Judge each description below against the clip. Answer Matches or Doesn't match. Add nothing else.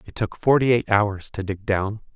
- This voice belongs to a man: Matches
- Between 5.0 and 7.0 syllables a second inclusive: Doesn't match